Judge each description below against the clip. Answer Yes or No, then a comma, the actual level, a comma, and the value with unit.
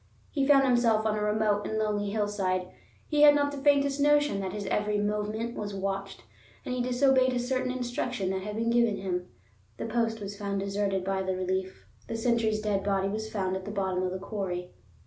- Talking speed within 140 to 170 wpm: No, fast, 205 wpm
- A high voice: Yes, high, 210 Hz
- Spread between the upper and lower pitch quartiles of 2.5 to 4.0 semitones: Yes, average, 3.7 semitones